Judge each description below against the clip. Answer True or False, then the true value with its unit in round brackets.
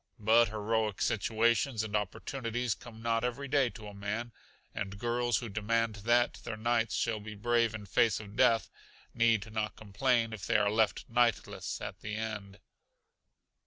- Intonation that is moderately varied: False (1.9 semitones)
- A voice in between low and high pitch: False (110 Hz)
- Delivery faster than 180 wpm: False (160 wpm)